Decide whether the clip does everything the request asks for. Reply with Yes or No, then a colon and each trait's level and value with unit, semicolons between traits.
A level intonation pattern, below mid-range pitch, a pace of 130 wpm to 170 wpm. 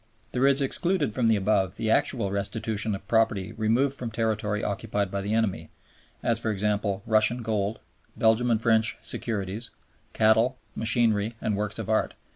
Yes: narrow, 2.0 semitones; low, 110 Hz; average, 160 wpm